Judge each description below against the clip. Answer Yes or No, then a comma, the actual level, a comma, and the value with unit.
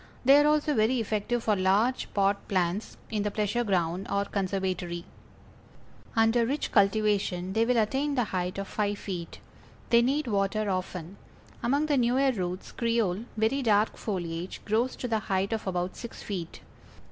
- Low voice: No, high, 210 Hz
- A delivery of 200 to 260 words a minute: No, average, 160 wpm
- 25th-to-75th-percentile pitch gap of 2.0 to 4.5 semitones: Yes, average, 3.8 semitones